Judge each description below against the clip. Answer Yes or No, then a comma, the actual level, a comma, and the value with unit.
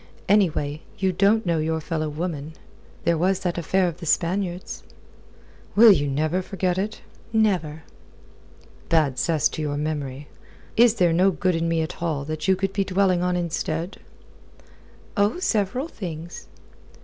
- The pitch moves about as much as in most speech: Yes, average, 3.6 semitones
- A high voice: No, medium, 175 Hz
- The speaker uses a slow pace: No, average, 150 wpm